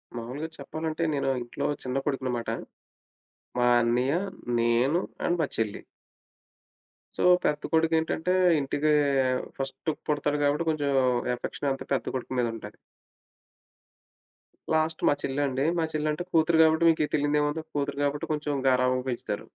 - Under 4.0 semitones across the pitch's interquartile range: Yes, average, 3.4 semitones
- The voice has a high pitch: No, medium, 145 Hz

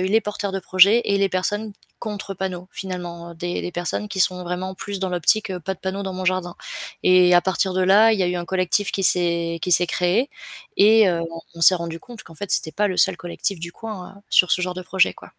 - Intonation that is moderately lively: No, narrow, 2.1 semitones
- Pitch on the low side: No, medium, 185 Hz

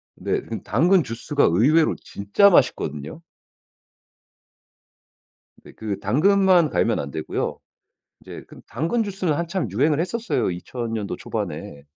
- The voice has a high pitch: No, medium, 145 Hz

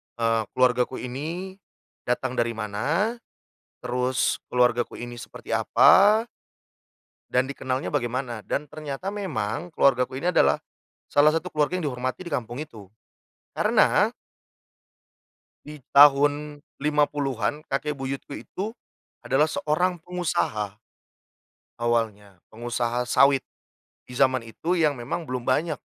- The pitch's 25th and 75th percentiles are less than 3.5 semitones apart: No, average, 4.1 semitones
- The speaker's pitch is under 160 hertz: Yes, low, 135 Hz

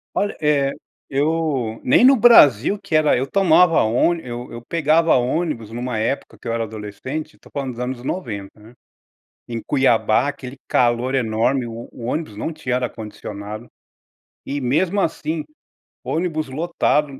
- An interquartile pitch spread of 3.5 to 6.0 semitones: Yes, average, 5.0 semitones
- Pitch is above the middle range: No, low, 130 Hz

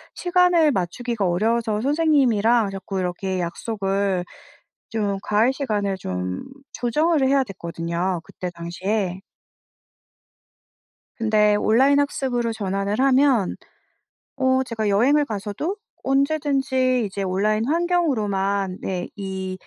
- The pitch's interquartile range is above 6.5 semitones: No, wide, 5.6 semitones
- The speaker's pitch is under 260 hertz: Yes, high, 215 Hz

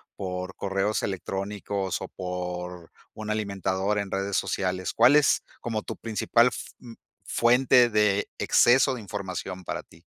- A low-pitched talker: Yes, low, 100 Hz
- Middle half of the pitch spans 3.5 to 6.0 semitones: No, average, 2.9 semitones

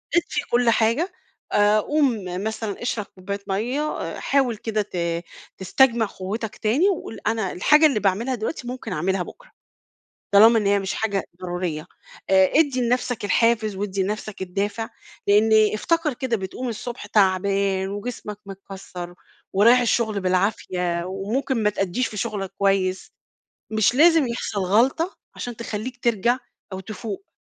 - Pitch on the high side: Yes, high, 215 Hz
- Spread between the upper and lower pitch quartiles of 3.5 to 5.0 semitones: Yes, average, 3.8 semitones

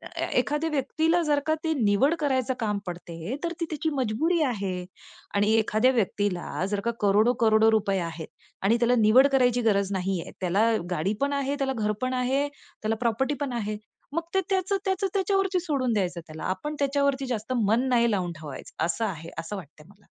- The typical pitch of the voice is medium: No, high, 230 Hz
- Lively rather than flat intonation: Yes, wide, 5.9 semitones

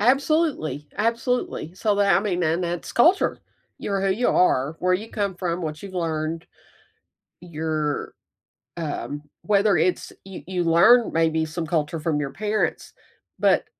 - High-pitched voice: No, medium, 180 Hz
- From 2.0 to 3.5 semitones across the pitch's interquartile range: No, average, 4.6 semitones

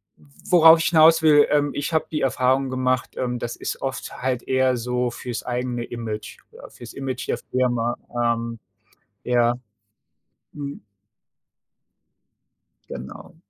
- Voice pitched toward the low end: Yes, low, 125 Hz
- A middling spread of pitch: Yes, average, 3.0 semitones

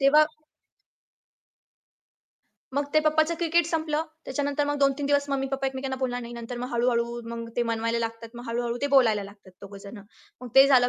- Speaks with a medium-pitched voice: No, very high, 260 Hz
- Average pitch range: Yes, average, 3.5 semitones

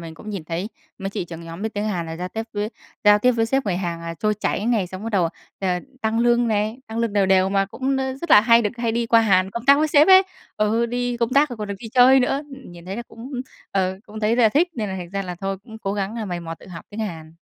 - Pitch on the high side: Yes, high, 210 Hz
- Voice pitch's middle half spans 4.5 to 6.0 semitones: No, average, 3.9 semitones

